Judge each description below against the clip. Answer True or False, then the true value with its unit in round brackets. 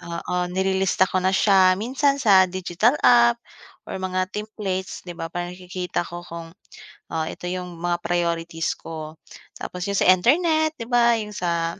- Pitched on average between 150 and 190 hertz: True (185 Hz)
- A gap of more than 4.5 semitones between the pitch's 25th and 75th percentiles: False (3.4 semitones)